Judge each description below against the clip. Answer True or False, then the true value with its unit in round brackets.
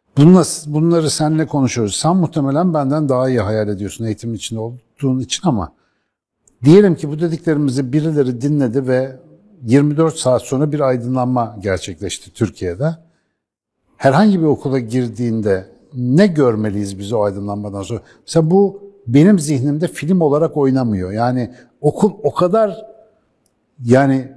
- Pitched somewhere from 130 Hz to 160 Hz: True (135 Hz)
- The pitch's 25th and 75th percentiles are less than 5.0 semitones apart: False (5.3 semitones)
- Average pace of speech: True (125 wpm)